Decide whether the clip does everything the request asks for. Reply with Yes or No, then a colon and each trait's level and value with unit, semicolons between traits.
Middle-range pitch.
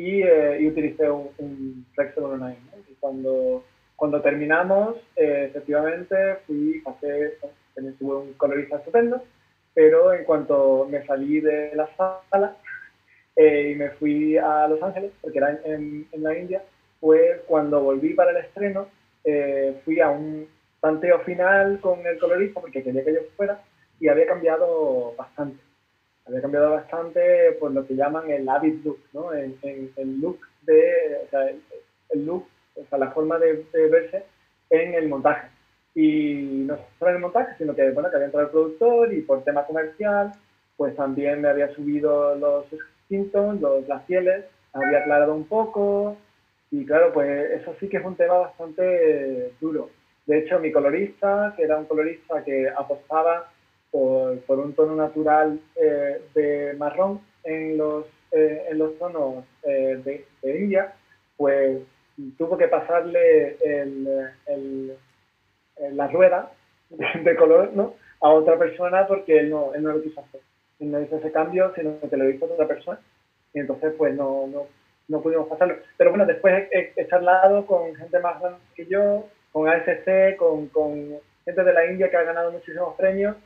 Yes: medium, 155 Hz